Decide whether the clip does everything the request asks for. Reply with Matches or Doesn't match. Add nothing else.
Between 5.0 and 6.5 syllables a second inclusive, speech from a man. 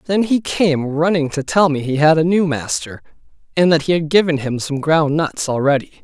Matches